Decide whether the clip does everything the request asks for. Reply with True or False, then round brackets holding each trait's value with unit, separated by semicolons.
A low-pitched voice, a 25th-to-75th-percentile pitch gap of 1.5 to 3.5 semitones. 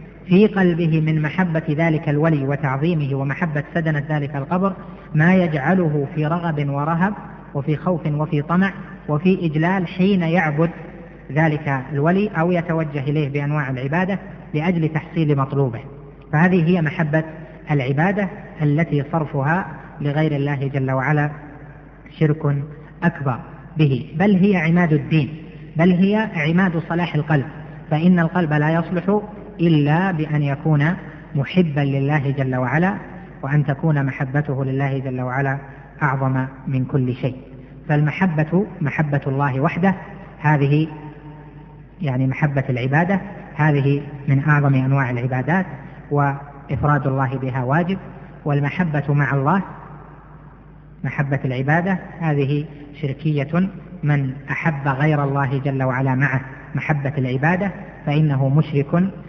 False (150 Hz; 3.1 semitones)